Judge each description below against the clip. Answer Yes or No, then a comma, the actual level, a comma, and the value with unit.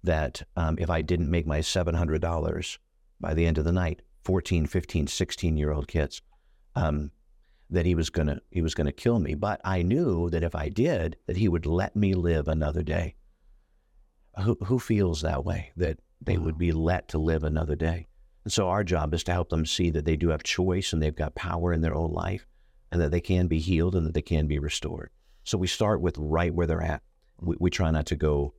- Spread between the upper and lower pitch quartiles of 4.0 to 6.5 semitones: No, average, 2.7 semitones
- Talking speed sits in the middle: No, fast, 230 wpm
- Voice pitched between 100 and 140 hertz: No, very low, 85 Hz